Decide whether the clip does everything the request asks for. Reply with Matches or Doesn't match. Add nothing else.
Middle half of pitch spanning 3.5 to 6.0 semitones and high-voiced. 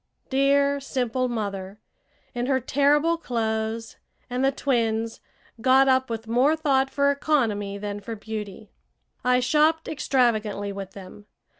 Matches